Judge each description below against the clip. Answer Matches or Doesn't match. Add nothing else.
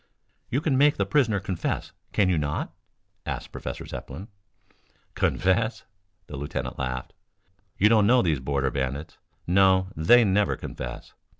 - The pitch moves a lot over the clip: Matches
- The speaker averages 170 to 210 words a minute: Doesn't match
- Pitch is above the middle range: Doesn't match